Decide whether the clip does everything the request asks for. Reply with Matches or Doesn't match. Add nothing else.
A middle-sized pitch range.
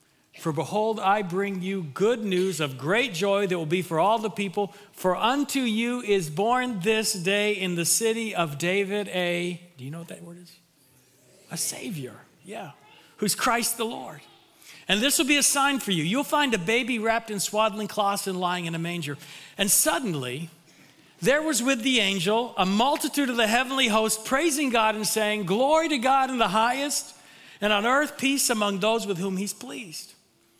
Matches